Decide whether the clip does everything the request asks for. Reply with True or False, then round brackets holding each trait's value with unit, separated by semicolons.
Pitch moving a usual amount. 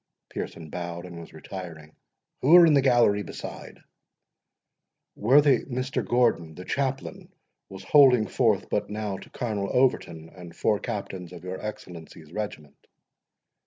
False (6.4 semitones)